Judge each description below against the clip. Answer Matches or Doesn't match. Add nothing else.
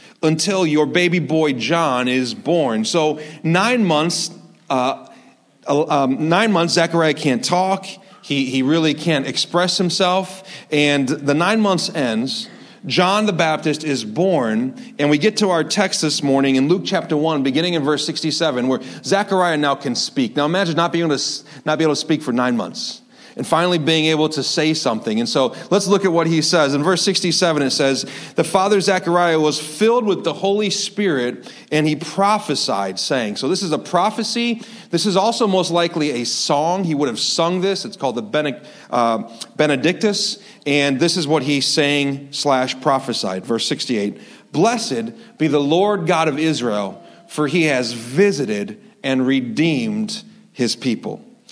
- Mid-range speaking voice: Matches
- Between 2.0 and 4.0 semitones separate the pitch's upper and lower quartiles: Doesn't match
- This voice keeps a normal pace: Matches